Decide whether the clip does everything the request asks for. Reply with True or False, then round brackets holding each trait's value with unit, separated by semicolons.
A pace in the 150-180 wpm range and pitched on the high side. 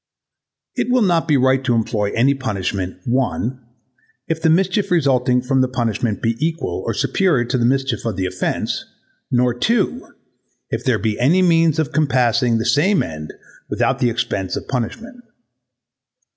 False (160 wpm; 130 Hz)